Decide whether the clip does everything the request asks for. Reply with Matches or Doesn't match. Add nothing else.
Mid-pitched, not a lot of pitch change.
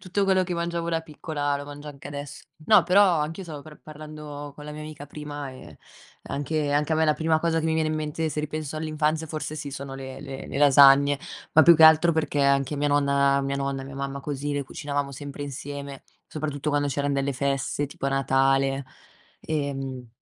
Matches